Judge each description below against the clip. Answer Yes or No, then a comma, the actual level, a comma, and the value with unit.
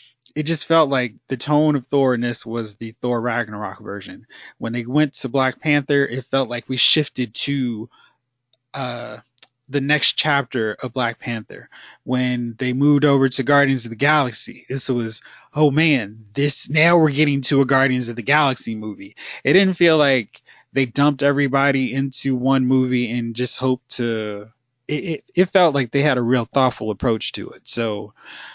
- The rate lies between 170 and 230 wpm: Yes, average, 180 wpm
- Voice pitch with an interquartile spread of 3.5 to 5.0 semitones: No, average, 3.1 semitones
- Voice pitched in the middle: No, low, 130 Hz